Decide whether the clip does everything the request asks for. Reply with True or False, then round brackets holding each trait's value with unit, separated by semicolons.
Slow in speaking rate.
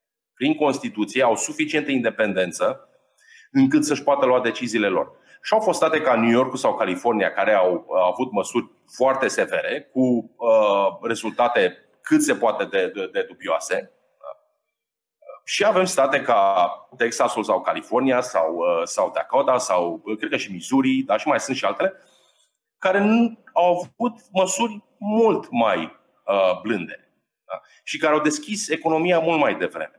False (155 wpm)